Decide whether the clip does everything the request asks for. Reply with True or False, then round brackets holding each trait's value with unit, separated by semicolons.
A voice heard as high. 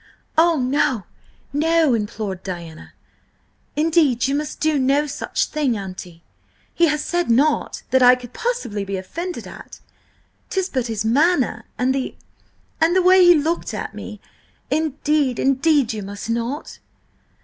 True (275 Hz)